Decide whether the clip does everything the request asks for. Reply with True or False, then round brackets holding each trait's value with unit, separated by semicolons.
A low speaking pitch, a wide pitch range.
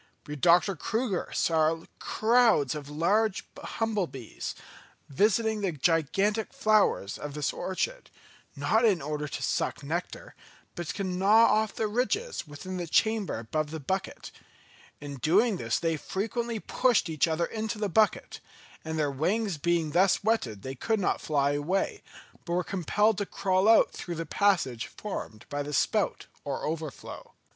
False (180 Hz; 6.1 semitones)